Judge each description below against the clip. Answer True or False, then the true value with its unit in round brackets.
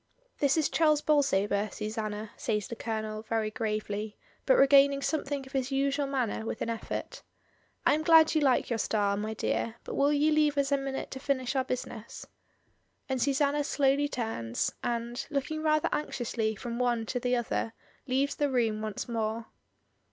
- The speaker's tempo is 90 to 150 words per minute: False (175 wpm)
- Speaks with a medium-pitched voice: False (250 Hz)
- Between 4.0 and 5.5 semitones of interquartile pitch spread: True (4.3 semitones)